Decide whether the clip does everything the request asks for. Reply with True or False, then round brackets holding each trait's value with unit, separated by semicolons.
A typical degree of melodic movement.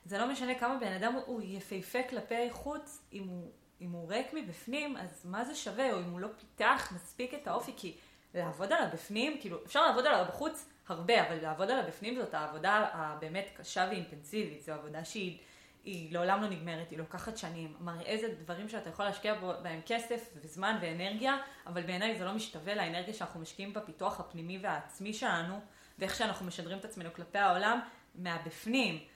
True (4.7 semitones)